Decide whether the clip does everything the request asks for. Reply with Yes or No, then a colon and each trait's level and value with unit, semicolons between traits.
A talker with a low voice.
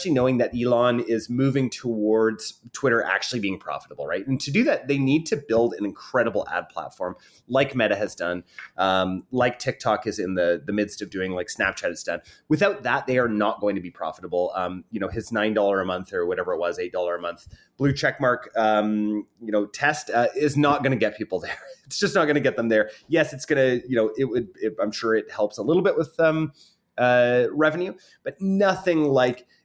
Yes: low, 120 Hz